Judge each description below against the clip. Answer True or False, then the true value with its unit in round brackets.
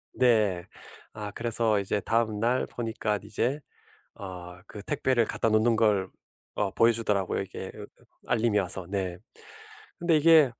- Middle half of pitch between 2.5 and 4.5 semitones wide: True (2.9 semitones)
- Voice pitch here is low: True (110 Hz)